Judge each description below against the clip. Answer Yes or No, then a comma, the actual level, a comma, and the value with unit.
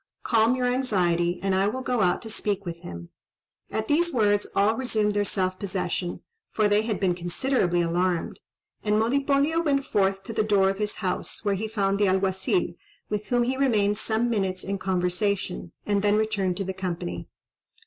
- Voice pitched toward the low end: No, high, 205 Hz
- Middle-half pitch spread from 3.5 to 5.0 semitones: No, average, 3.1 semitones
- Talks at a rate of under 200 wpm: Yes, average, 185 wpm